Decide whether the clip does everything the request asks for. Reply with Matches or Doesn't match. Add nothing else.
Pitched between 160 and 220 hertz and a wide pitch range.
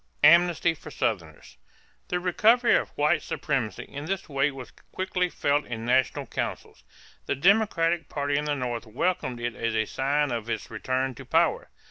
Doesn't match